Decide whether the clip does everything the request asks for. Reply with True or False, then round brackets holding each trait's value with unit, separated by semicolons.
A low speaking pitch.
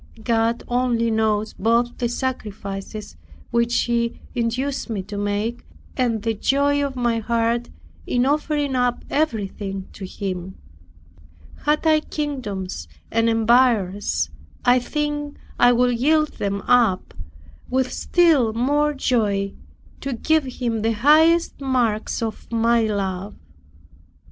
False (235 Hz)